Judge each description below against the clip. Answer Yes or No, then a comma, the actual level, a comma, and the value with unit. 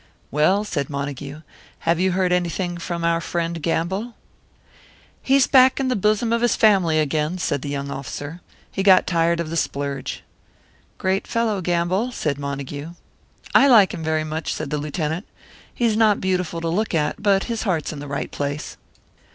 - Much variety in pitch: No, average, 4.7 semitones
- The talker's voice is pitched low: No, medium, 170 Hz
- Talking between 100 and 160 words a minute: No, average, 175 wpm